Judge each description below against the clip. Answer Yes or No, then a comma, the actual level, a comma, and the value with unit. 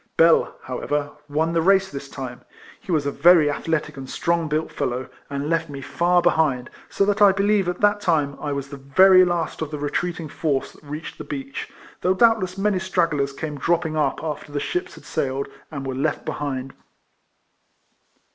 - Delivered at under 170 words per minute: No, average, 195 wpm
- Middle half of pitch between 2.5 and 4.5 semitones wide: Yes, average, 4.1 semitones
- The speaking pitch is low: No, medium, 155 Hz